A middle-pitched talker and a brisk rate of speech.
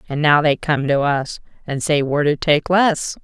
Yes: medium, 150 Hz; fast, 225 wpm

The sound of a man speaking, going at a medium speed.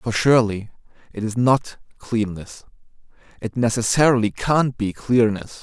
No: male; slow, 105 wpm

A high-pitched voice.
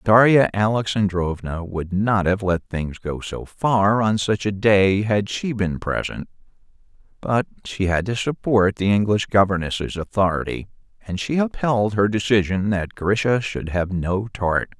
No: low, 100 Hz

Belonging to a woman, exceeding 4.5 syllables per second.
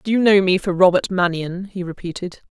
Yes: female; 5.4 syllables/s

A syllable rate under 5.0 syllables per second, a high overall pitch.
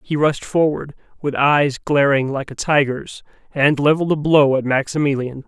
No: 4.8 syllables/s; medium, 140 Hz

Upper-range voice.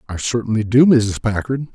No: low, 115 Hz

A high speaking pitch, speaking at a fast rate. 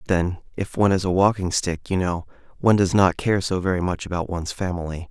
No: very low, 90 Hz; fast, 235 wpm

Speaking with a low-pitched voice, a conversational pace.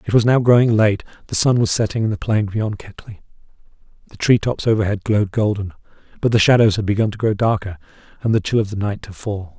No: low, 105 Hz; fast, 225 wpm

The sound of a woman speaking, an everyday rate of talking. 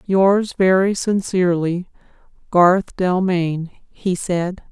No: female; slow, 90 wpm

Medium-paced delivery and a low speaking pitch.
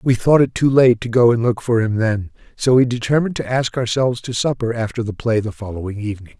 No: fast, 245 wpm; low, 120 Hz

